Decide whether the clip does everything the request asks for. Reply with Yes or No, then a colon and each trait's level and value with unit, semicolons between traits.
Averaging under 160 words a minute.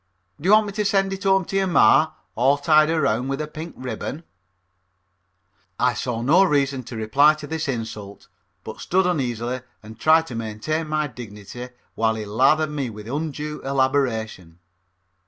No: average, 170 wpm